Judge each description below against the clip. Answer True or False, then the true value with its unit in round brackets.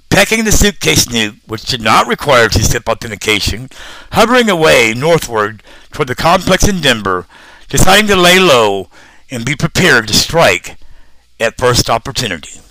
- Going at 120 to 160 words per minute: True (140 wpm)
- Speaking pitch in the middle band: False (120 Hz)